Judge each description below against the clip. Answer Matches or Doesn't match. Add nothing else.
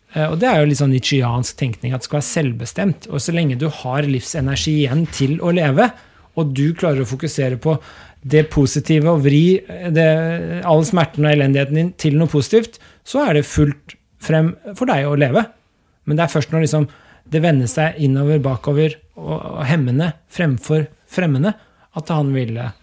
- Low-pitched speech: Doesn't match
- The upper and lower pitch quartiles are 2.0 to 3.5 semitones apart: Matches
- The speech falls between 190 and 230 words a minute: Doesn't match